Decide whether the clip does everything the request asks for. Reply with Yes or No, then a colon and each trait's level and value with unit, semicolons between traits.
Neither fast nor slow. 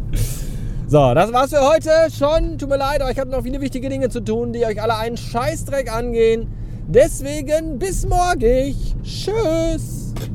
Yes: average, 160 wpm